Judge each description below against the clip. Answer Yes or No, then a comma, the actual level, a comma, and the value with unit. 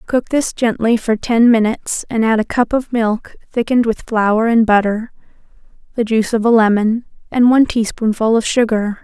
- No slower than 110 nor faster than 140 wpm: No, average, 180 wpm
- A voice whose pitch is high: Yes, high, 225 Hz